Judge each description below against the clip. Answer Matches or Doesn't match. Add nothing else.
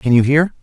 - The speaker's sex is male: Matches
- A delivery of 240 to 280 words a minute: Doesn't match